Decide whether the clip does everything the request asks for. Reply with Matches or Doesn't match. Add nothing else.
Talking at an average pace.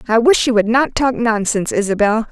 Doesn't match